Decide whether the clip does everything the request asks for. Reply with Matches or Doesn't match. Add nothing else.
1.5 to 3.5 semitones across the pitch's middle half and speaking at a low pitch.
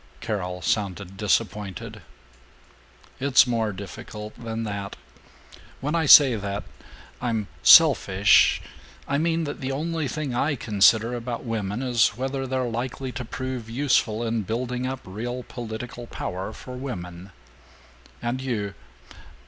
Doesn't match